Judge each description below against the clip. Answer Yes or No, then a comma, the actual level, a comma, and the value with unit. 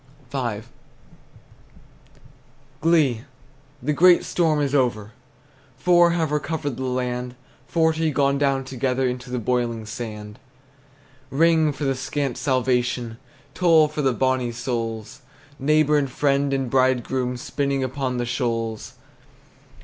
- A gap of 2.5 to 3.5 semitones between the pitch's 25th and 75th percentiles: Yes, average, 3.1 semitones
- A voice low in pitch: Yes, low, 130 Hz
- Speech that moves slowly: Yes, slow, 120 wpm